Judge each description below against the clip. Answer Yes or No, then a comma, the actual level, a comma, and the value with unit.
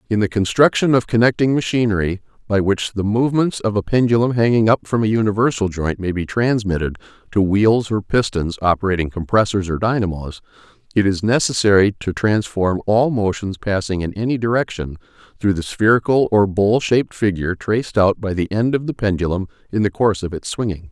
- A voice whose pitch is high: No, low, 105 Hz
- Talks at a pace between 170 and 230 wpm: Yes, average, 180 wpm